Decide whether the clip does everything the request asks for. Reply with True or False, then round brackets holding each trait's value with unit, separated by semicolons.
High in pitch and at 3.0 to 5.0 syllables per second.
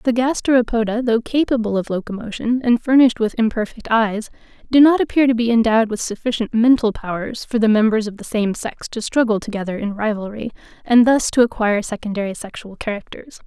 False (225 Hz; 5.9 syllables/s)